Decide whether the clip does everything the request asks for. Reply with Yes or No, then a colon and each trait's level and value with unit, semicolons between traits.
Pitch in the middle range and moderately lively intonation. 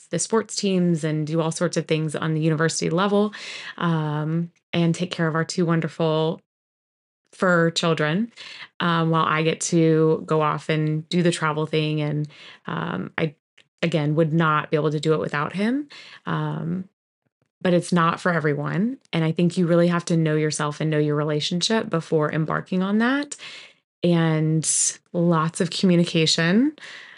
No: medium, 165 Hz; narrow, 2.2 semitones